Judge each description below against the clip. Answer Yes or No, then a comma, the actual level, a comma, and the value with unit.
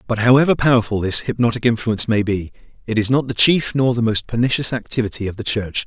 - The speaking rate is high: Yes, fast, 215 wpm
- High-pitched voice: No, low, 115 Hz